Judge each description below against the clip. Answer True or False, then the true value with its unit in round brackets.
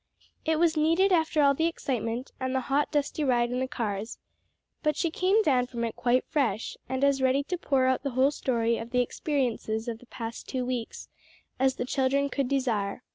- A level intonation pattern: False (3.3 semitones)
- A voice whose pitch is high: True (260 Hz)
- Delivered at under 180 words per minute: False (205 wpm)